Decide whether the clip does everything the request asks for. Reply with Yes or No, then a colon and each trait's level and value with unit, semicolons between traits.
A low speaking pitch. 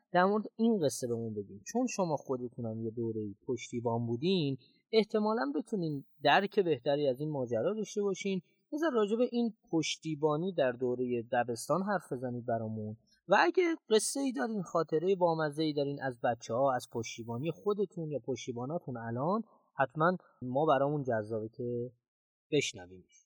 No: medium, 150 Hz